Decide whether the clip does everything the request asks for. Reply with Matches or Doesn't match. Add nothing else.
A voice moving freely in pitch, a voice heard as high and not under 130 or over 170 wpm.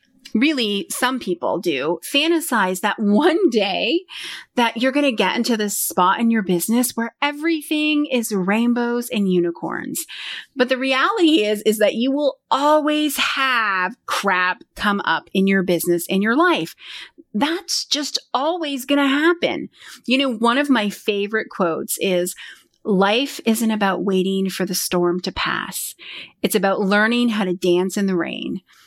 Matches